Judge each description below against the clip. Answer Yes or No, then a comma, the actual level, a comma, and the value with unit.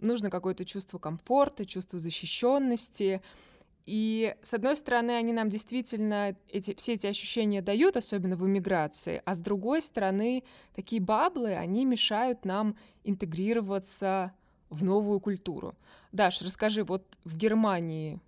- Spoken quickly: No, average, 130 wpm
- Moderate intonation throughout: Yes, average, 3.6 semitones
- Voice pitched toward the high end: Yes, high, 205 Hz